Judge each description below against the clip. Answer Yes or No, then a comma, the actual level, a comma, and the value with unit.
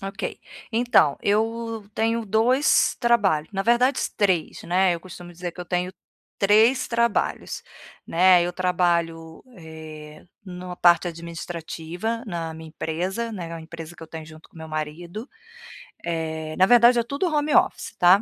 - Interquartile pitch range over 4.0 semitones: Yes, average, 5.2 semitones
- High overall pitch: No, medium, 180 Hz